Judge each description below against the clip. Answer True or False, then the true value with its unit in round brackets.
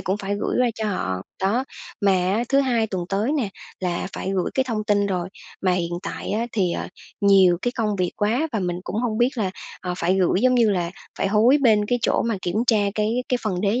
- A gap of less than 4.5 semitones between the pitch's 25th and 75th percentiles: True (3.9 semitones)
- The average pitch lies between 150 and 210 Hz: True (205 Hz)